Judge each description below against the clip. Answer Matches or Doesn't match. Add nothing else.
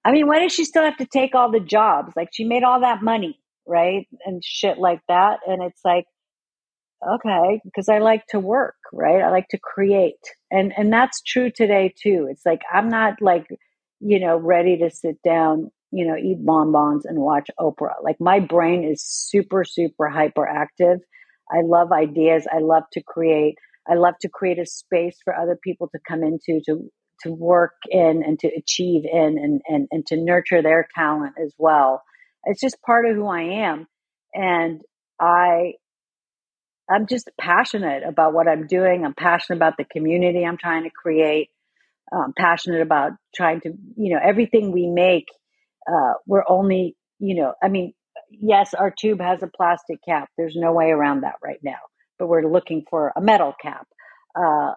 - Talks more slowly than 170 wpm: Doesn't match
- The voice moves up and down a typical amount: Matches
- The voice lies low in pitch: Doesn't match